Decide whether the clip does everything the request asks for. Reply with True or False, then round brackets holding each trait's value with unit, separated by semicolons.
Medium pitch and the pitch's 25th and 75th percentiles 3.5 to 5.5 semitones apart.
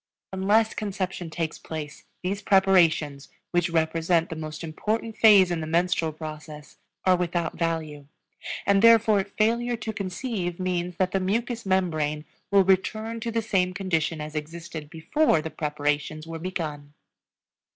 True (175 Hz; 4.0 semitones)